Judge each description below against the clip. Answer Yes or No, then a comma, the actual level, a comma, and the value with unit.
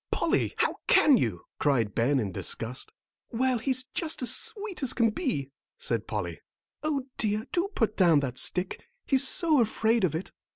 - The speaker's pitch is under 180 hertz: No, high, 225 Hz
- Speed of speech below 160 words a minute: No, average, 170 wpm